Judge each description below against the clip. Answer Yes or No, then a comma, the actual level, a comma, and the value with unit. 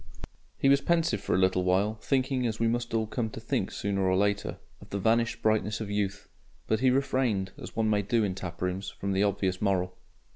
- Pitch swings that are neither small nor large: Yes, average, 3.4 semitones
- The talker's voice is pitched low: Yes, low, 105 Hz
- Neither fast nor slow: No, fast, 215 wpm